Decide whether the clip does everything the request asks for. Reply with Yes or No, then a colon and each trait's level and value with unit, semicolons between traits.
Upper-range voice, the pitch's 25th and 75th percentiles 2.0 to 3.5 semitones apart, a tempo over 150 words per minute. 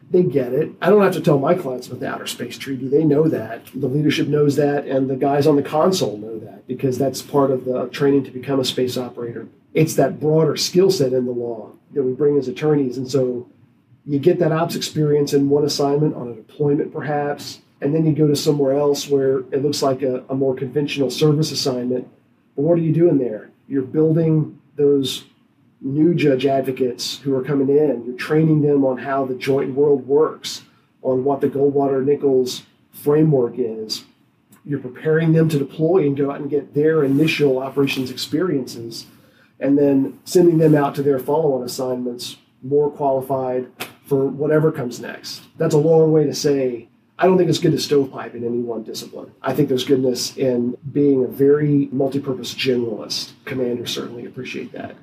No: medium, 140 Hz; narrow, 2.4 semitones; average, 190 wpm